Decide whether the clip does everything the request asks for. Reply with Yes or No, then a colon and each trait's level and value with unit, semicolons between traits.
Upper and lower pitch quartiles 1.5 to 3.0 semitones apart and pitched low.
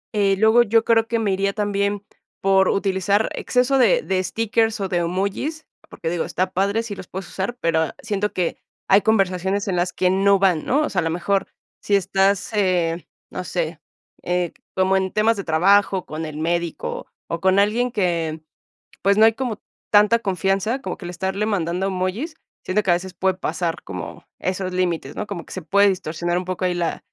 No: narrow, 2.6 semitones; high, 190 Hz